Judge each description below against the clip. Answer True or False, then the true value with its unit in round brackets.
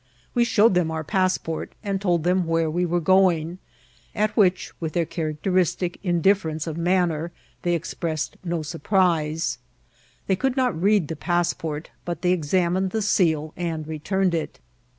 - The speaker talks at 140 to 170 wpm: True (160 wpm)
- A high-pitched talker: False (175 Hz)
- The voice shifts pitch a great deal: False (2.8 semitones)